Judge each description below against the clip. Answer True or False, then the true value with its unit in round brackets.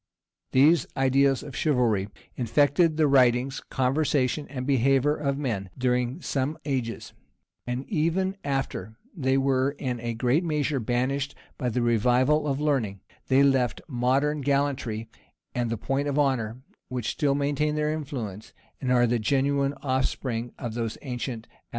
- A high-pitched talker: False (135 Hz)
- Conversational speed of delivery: True (150 wpm)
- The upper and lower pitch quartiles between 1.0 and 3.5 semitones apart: True (2.8 semitones)